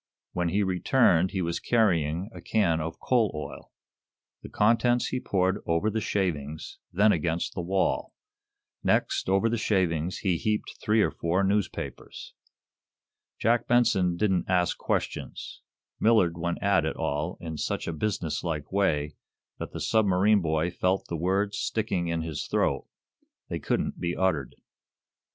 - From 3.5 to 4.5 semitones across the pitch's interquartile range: Yes, average, 4.0 semitones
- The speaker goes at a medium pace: Yes, average, 150 wpm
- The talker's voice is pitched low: Yes, very low, 90 Hz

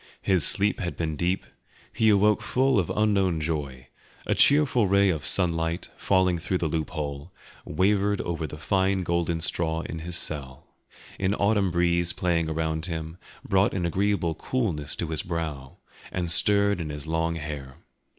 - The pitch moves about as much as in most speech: Yes, average, 3.5 semitones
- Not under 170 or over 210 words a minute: No, average, 160 wpm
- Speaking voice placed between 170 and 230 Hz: No, very low, 85 Hz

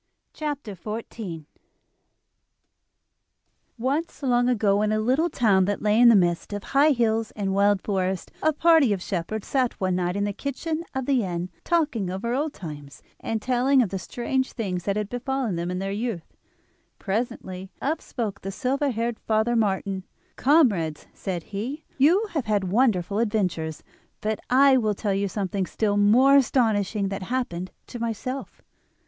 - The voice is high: Yes, high, 215 Hz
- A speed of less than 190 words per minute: Yes, average, 165 wpm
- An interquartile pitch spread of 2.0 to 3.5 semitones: No, average, 4.9 semitones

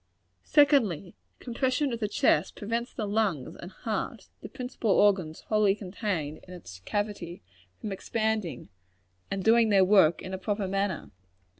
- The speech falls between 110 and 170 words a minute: Yes, average, 145 wpm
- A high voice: Yes, high, 205 Hz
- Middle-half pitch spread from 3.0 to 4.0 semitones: Yes, average, 3.3 semitones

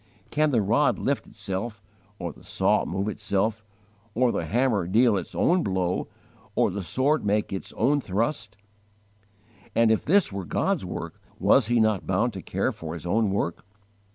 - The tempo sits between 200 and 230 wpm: No, average, 170 wpm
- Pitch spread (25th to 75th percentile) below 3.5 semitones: No, average, 4.0 semitones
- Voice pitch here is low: Yes, low, 105 Hz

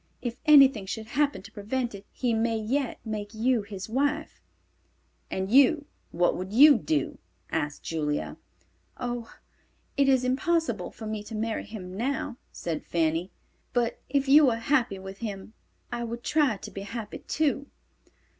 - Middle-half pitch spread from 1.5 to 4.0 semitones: No, average, 5.0 semitones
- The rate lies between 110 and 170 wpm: Yes, average, 155 wpm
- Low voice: No, high, 230 Hz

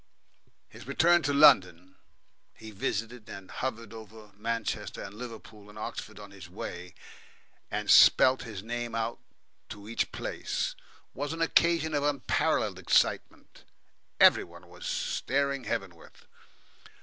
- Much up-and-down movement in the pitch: No, average, 4.8 semitones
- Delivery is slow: Yes, slow, 125 wpm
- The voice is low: Yes, low, 110 Hz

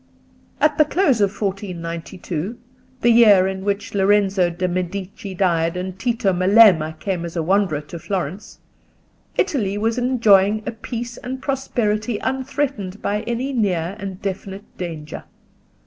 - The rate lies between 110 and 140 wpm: Yes, slow, 135 wpm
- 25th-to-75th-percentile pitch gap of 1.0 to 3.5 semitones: No, average, 4.0 semitones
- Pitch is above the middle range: Yes, high, 200 Hz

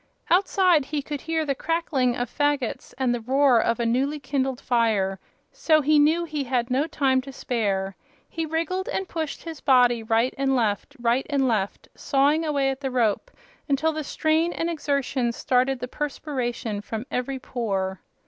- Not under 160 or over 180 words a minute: Yes, average, 175 wpm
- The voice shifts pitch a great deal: No, average, 4.0 semitones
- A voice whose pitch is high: Yes, very high, 270 Hz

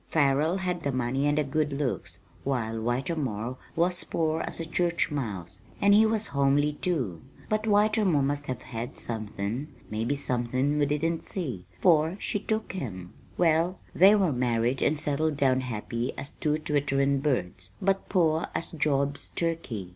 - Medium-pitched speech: Yes, medium, 145 Hz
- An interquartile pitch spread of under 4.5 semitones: No, average, 4.9 semitones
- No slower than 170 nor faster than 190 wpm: No, average, 155 wpm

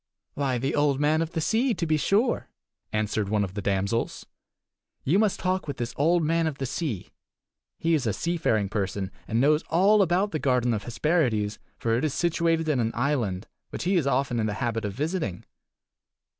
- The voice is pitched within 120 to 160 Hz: Yes, medium, 140 Hz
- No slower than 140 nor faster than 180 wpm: No, average, 200 wpm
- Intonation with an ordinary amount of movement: No, wide, 6.8 semitones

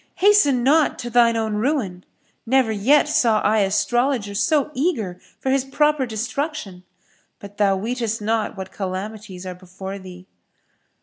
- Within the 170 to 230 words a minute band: No, average, 140 wpm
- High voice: Yes, high, 220 Hz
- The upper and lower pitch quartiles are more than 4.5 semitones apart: Yes, average, 5.2 semitones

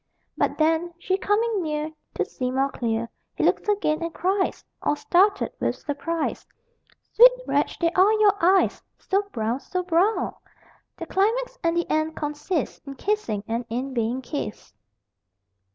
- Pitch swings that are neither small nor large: No, wide, 6.1 semitones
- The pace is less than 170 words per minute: Yes, average, 155 wpm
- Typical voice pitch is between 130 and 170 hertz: No, very high, 335 Hz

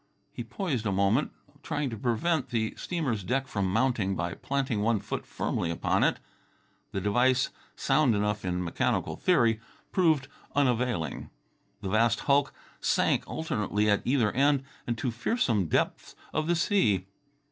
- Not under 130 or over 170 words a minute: Yes, average, 145 wpm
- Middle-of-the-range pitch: No, low, 120 Hz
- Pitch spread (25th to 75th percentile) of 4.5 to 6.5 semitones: Yes, average, 5.1 semitones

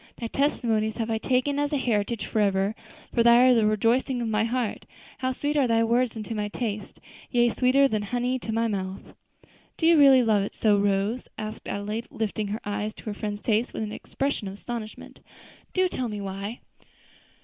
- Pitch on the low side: No, high, 225 Hz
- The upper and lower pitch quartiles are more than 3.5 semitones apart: No, average, 3.2 semitones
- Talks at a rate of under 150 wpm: No, average, 195 wpm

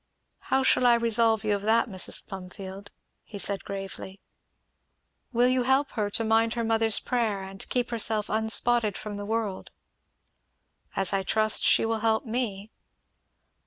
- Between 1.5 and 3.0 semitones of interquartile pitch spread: Yes, narrow, 2.5 semitones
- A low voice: No, high, 220 Hz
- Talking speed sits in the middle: Yes, average, 155 wpm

